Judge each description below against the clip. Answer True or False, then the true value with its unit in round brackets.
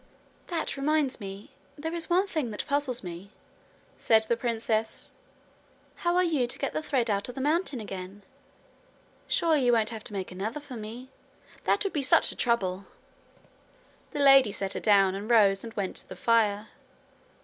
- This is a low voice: False (235 Hz)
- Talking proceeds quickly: False (180 wpm)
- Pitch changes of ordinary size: False (5.8 semitones)